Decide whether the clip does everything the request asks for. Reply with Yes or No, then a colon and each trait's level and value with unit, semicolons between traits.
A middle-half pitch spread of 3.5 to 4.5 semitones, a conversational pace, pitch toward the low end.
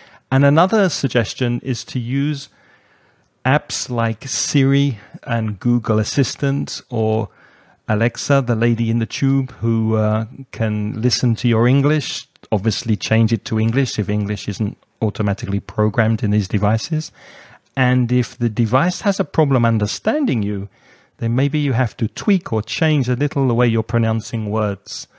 Yes: average, 3.8 semitones; average, 150 wpm; low, 115 Hz